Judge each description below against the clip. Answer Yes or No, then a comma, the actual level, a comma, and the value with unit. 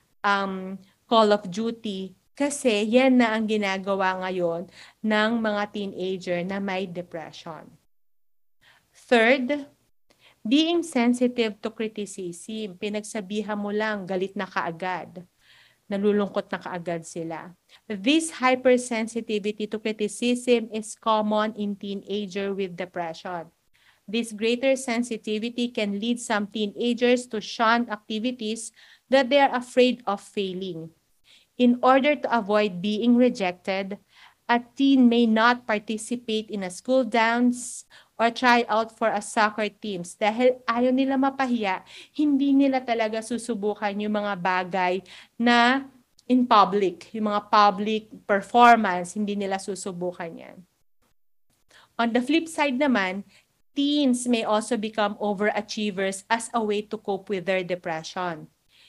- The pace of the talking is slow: No, average, 120 wpm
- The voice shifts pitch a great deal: No, average, 3.5 semitones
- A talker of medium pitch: No, high, 215 Hz